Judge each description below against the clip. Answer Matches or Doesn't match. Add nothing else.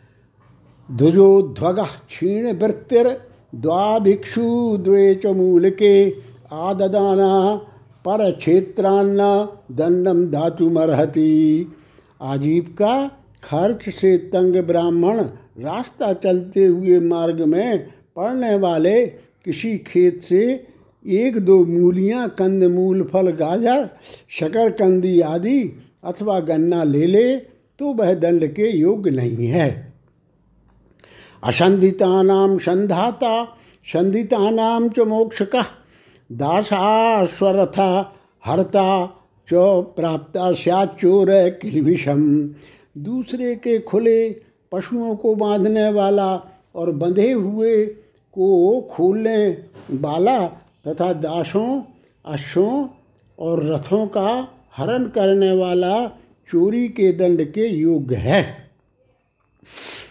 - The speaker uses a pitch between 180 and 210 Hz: Matches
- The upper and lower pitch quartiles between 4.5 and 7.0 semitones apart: Doesn't match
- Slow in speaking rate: Matches